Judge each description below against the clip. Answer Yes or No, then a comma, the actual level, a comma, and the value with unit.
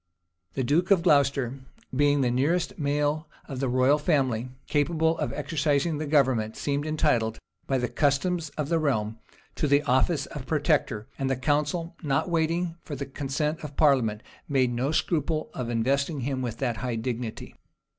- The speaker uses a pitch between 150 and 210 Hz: No, medium, 140 Hz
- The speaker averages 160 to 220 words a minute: Yes, average, 170 wpm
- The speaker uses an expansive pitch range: No, average, 3.4 semitones